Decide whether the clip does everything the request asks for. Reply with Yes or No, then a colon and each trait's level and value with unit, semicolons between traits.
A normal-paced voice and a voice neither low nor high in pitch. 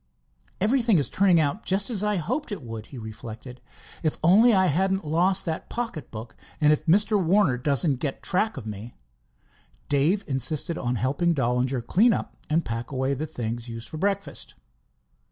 Yes: average, 170 wpm; medium, 155 Hz